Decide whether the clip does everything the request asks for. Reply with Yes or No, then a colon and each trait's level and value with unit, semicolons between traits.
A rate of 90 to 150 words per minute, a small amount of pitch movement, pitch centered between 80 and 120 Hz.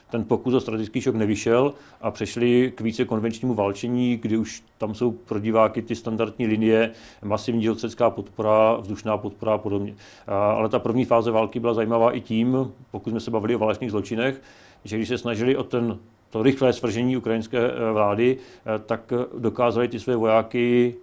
No: fast, 170 wpm; narrow, 1.8 semitones; low, 115 Hz